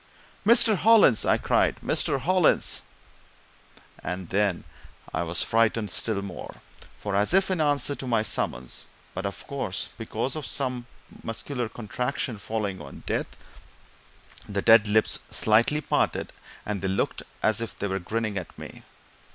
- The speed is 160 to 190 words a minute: No, average, 145 wpm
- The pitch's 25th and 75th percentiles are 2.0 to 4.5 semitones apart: No, average, 5.1 semitones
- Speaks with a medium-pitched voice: No, low, 110 Hz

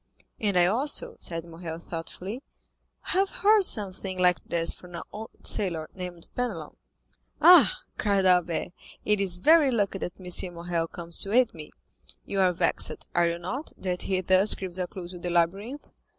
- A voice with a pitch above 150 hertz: Yes, medium, 185 Hz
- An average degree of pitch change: Yes, average, 3.5 semitones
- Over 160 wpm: Yes, average, 170 wpm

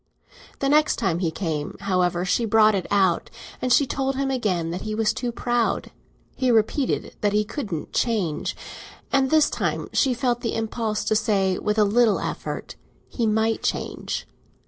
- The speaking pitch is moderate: No, high, 220 Hz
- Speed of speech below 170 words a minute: No, average, 175 wpm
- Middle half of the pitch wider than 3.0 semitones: Yes, average, 3.9 semitones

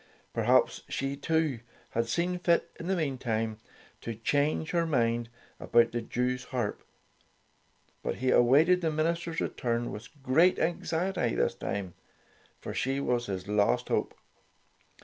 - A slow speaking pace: Yes, slow, 130 wpm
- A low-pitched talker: Yes, low, 130 Hz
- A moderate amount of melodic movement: No, wide, 5.8 semitones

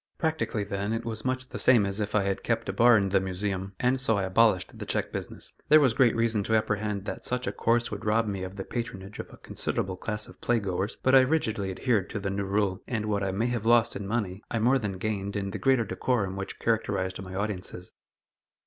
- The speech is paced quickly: Yes, fast, 240 wpm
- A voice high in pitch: No, low, 105 Hz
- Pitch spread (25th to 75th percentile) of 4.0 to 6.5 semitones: No, average, 3.1 semitones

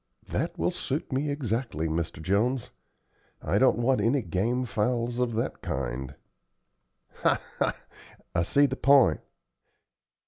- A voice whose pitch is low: Yes, low, 115 Hz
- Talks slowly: Yes, slow, 130 wpm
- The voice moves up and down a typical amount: No, wide, 6.0 semitones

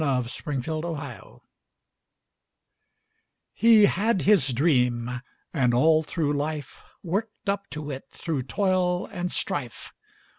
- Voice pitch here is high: No, medium, 155 Hz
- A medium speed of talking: No, slow, 115 wpm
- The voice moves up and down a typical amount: No, wide, 5.8 semitones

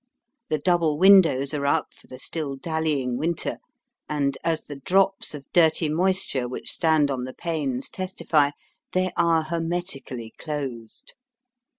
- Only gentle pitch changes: No, average, 3.6 semitones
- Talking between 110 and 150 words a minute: Yes, slow, 135 wpm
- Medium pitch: Yes, medium, 155 Hz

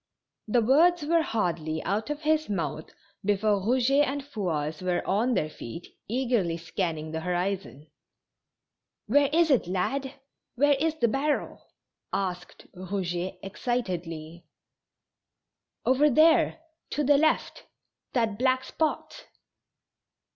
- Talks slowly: Yes, slow, 120 wpm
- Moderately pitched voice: No, high, 215 Hz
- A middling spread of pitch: No, wide, 7.9 semitones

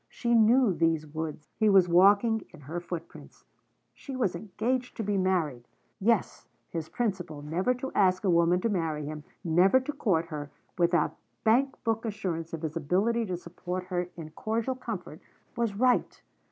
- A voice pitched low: No, medium, 185 Hz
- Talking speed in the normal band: Yes, average, 165 wpm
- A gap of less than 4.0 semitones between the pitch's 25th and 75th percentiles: No, average, 5.3 semitones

